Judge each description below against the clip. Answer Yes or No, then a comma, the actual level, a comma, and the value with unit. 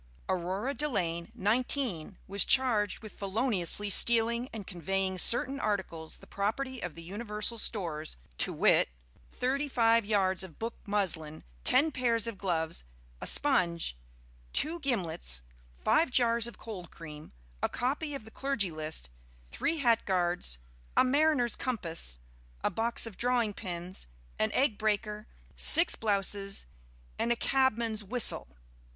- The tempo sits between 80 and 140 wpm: Yes, slow, 135 wpm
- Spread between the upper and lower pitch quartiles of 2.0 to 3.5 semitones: No, average, 5.2 semitones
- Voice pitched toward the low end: No, high, 210 Hz